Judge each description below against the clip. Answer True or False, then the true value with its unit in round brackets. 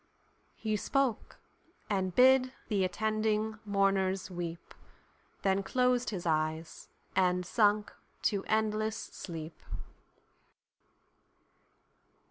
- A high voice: True (200 Hz)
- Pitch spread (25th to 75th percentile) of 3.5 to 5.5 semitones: False (3.1 semitones)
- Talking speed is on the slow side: True (80 wpm)